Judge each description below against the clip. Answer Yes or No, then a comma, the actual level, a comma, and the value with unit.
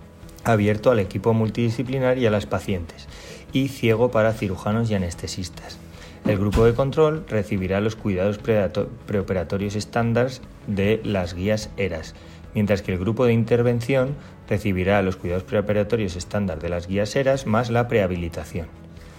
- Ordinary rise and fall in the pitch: Yes, average, 3.9 semitones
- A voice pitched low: Yes, low, 105 Hz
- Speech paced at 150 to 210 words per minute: No, average, 140 wpm